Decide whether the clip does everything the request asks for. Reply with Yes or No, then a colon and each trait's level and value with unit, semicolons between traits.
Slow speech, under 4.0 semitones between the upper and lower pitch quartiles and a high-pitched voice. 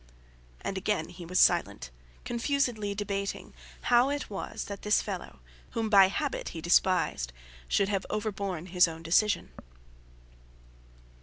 Yes: slow, 130 wpm; average, 2.9 semitones; high, 200 Hz